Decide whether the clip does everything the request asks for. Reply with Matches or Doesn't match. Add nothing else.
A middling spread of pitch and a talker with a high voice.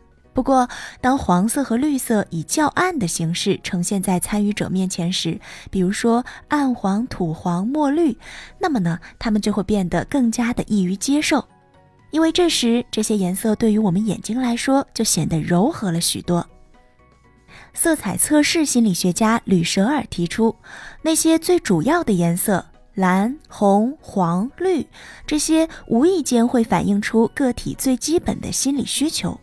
Doesn't match